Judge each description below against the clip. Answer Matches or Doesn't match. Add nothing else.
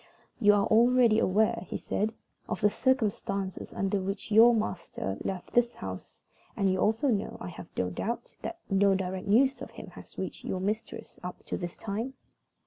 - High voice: Matches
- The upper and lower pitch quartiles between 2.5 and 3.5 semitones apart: Matches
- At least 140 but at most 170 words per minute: Doesn't match